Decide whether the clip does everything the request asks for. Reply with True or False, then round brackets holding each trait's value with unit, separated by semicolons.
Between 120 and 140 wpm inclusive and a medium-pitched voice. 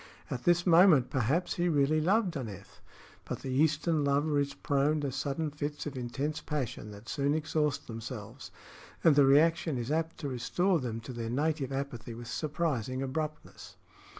False (165 wpm; 145 Hz)